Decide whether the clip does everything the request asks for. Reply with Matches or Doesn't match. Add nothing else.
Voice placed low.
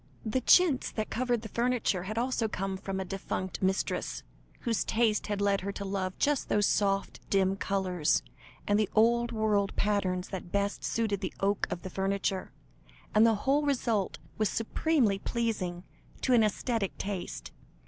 Doesn't match